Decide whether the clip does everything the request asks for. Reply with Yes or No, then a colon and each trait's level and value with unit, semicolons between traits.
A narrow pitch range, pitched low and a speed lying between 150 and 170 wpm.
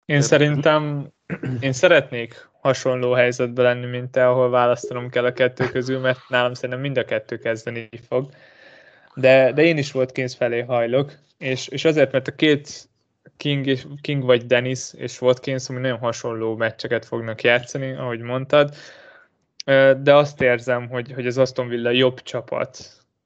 Yes: narrow, 1.7 semitones; low, 130 Hz; fast, 155 wpm